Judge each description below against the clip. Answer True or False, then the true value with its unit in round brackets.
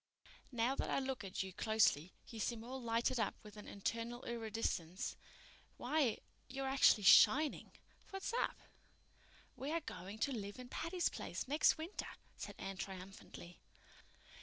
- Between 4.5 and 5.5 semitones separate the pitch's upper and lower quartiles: True (4.9 semitones)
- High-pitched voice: True (230 Hz)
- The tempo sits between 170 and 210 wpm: False (145 wpm)